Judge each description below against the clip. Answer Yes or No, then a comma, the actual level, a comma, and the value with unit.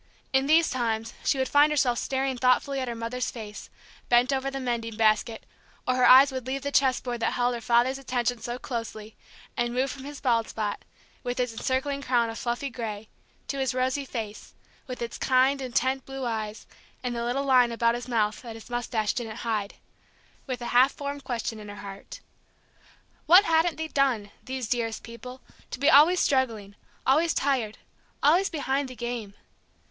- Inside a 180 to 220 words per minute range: Yes, average, 185 wpm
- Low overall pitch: No, very high, 250 Hz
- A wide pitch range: No, average, 2.7 semitones